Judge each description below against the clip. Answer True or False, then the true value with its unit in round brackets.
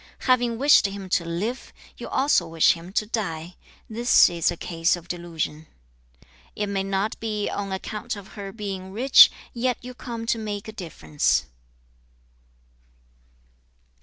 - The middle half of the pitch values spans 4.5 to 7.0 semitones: True (4.8 semitones)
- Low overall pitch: False (200 Hz)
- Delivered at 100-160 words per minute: True (150 wpm)